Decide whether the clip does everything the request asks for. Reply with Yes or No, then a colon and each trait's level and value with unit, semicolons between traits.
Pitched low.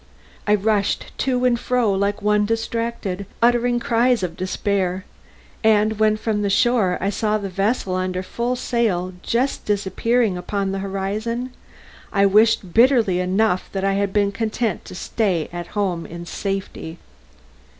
No: high, 205 Hz